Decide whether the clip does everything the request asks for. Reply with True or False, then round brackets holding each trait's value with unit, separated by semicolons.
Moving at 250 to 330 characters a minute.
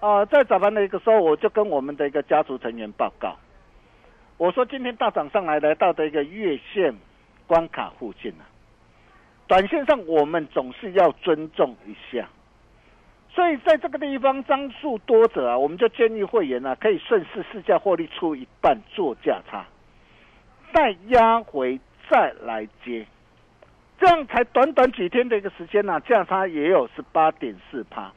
True (255 characters per minute)